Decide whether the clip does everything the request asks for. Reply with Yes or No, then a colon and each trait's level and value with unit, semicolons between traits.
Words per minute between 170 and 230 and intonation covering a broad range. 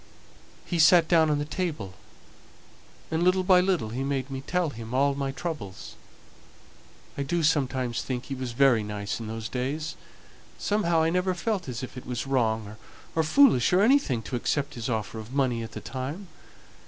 Yes: average, 180 wpm; wide, 5.9 semitones